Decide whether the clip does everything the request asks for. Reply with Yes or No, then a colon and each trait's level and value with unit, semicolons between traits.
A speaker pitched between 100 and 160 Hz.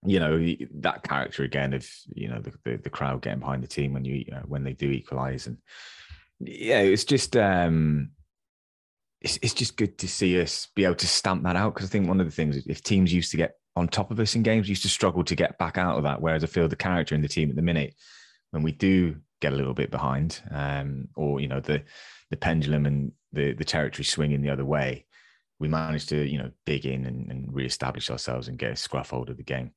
No: very low, 75 Hz